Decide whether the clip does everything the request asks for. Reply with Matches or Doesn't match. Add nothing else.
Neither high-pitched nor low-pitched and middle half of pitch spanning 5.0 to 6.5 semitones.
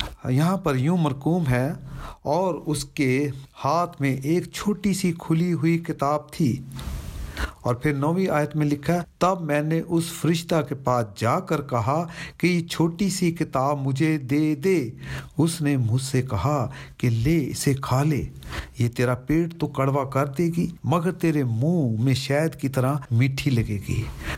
Doesn't match